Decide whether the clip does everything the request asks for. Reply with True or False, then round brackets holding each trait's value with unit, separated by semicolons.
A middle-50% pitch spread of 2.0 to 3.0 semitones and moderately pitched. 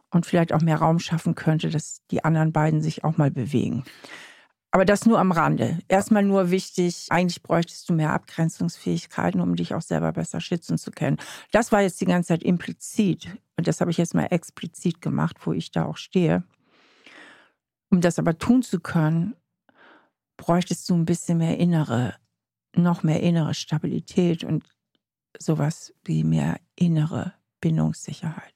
True (2.6 semitones; 170 Hz)